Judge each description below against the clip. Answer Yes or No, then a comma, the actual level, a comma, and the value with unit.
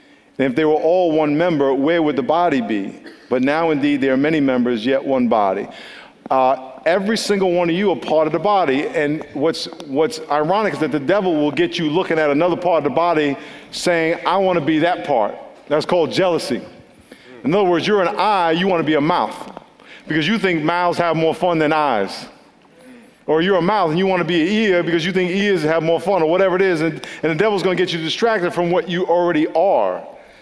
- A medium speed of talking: No, fast, 235 wpm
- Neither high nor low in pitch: Yes, medium, 165 Hz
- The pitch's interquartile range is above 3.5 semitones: No, average, 3.2 semitones